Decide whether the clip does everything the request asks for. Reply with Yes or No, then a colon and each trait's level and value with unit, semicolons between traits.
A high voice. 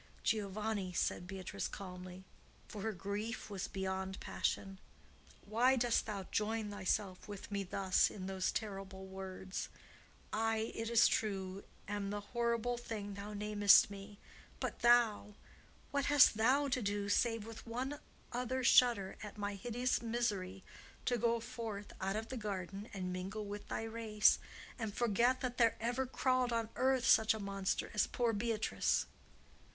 Yes: high, 210 Hz